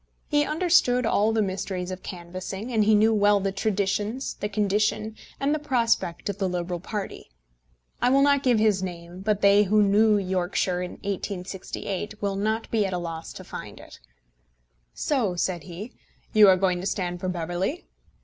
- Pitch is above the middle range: Yes, high, 200 Hz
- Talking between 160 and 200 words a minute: Yes, average, 180 wpm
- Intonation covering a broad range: No, average, 3.0 semitones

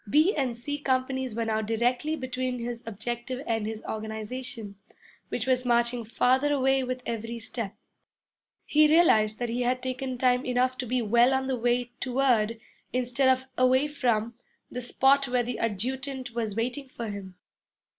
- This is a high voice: Yes, very high, 250 Hz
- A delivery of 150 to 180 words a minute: Yes, average, 165 wpm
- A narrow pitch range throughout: Yes, narrow, 2.3 semitones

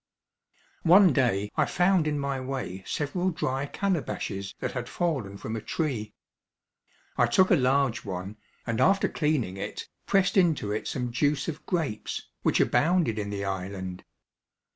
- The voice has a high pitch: No, low, 135 Hz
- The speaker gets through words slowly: No, average, 150 wpm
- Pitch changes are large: Yes, wide, 7.6 semitones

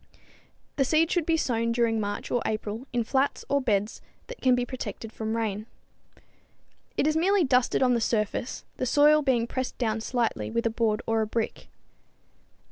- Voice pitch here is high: Yes, high, 235 Hz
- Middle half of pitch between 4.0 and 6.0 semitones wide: No, average, 3.3 semitones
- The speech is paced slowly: No, average, 180 wpm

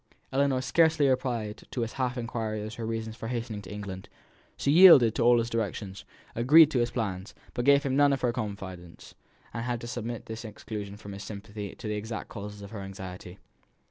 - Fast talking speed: Yes, fast, 210 wpm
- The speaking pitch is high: No, low, 115 Hz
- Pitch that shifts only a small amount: No, average, 3.3 semitones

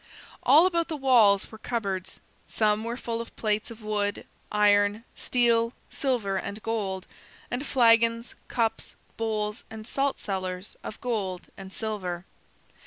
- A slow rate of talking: Yes, slow, 130 wpm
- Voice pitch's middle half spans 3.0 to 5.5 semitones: No, narrow, 2.5 semitones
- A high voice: Yes, high, 220 Hz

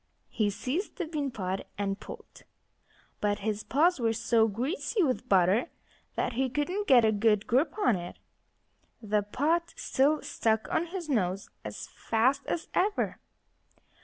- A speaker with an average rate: Yes, average, 150 wpm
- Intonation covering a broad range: Yes, wide, 6.7 semitones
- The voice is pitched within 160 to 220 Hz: No, high, 245 Hz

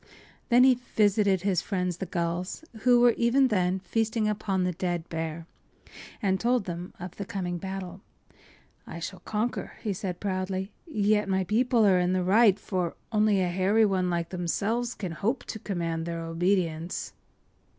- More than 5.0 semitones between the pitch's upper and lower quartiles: No, average, 3.1 semitones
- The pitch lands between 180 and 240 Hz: Yes, high, 190 Hz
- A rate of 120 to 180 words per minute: Yes, average, 170 wpm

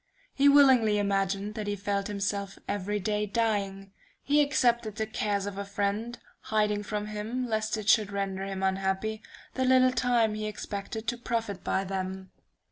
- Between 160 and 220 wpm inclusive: Yes, average, 165 wpm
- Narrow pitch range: Yes, narrow, 2.3 semitones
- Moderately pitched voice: No, high, 210 Hz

